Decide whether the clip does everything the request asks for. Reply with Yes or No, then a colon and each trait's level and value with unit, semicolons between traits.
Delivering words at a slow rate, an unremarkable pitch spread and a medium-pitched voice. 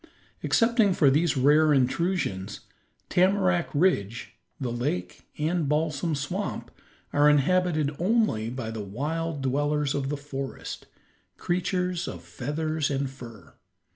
Yes: slow, 115 wpm; average, 4.7 semitones; medium, 145 Hz